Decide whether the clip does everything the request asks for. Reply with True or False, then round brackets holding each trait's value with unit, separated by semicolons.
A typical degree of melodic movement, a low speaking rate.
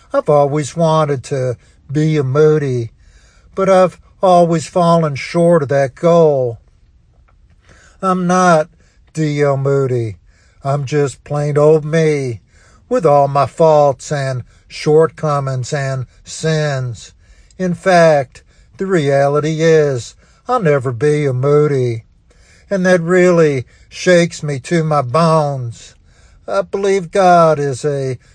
True (4.5 semitones; 115 wpm)